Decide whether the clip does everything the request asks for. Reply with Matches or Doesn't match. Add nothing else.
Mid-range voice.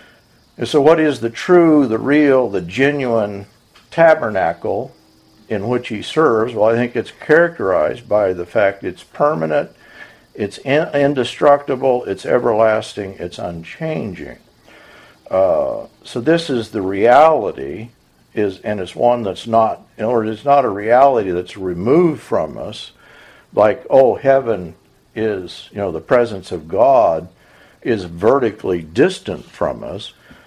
Doesn't match